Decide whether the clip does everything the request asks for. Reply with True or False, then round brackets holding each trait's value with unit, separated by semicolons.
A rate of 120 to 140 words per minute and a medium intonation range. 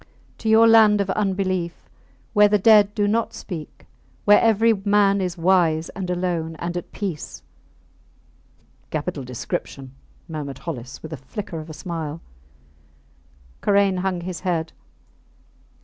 True (135 wpm; 4.1 semitones)